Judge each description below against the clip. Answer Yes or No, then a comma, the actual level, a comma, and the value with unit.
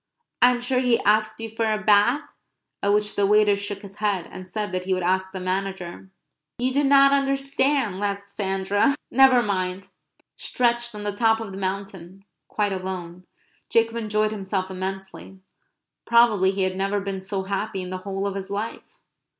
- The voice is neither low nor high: No, high, 200 Hz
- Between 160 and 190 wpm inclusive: Yes, average, 180 wpm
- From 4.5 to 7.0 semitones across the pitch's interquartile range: No, average, 2.8 semitones